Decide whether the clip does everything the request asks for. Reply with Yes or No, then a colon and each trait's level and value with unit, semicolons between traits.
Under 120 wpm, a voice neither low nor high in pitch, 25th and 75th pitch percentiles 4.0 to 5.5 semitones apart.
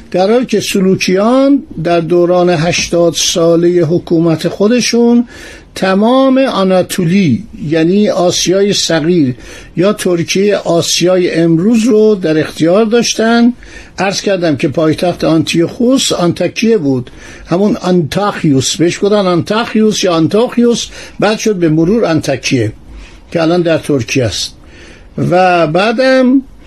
Yes: average, 110 wpm; medium, 180 Hz; average, 4.6 semitones